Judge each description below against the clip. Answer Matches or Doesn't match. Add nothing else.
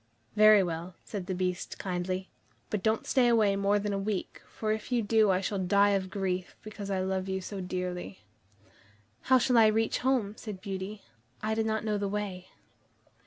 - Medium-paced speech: Matches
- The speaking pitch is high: Matches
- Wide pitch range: Doesn't match